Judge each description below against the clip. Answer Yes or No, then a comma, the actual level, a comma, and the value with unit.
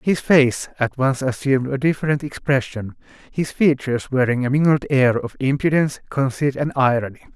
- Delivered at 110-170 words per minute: Yes, average, 155 wpm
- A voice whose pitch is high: No, low, 135 Hz